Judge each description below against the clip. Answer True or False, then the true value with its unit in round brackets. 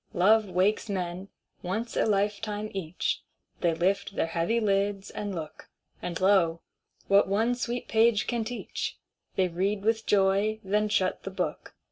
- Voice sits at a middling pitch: False (200 Hz)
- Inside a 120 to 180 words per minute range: True (150 wpm)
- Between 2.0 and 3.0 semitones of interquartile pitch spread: True (2.6 semitones)